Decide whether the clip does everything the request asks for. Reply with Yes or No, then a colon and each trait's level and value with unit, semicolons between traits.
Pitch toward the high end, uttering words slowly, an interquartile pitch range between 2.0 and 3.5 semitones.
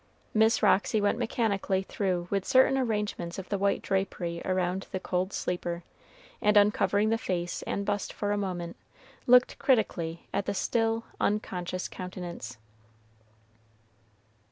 Yes: high, 195 Hz; slow, 130 wpm; average, 2.9 semitones